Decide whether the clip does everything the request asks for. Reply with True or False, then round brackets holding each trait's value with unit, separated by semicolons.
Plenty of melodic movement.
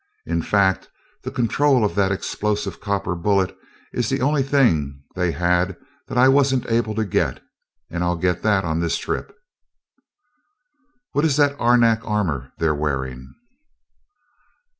True (5.9 semitones)